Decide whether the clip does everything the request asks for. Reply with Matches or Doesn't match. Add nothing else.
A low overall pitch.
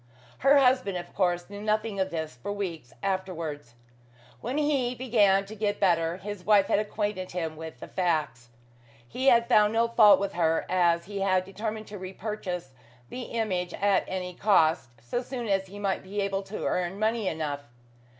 Doesn't match